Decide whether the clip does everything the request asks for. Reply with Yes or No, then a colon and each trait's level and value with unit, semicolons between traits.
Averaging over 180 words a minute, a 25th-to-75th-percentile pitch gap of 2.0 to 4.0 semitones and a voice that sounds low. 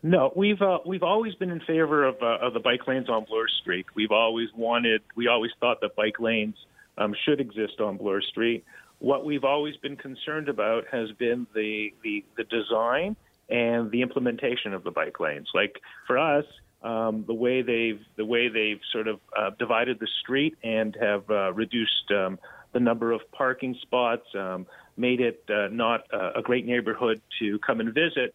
Yes: average, 190 wpm; average, 3.4 semitones; low, 120 Hz